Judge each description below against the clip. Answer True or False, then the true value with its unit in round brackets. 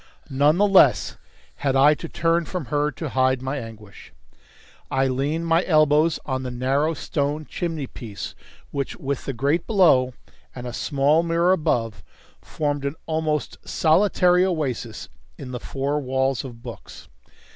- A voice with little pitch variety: False (3.7 semitones)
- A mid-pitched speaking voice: True (145 Hz)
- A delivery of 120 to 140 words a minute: False (150 wpm)